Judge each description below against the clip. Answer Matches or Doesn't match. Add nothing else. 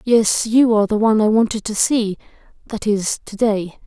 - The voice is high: Matches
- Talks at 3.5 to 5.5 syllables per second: Matches